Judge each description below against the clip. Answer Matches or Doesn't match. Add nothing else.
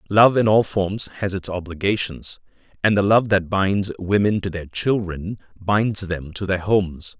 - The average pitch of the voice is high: Doesn't match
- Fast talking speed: Doesn't match